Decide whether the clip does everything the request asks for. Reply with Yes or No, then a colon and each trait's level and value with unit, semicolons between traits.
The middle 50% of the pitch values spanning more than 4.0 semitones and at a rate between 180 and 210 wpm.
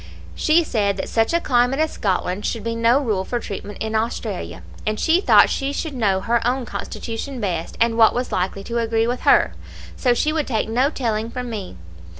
No: average, 3.2 semitones; fast, 205 wpm